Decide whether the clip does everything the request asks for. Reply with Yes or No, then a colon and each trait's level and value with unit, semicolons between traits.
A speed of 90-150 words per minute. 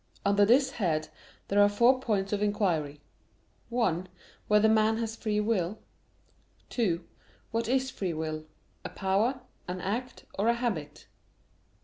Yes: slow, 135 wpm